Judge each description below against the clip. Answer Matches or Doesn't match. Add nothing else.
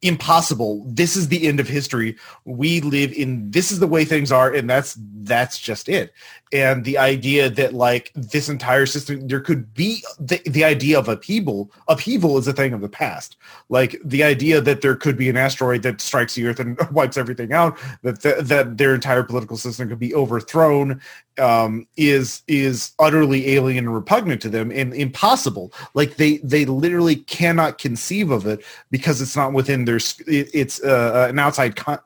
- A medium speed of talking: Matches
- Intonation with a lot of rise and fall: Doesn't match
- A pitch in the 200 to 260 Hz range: Doesn't match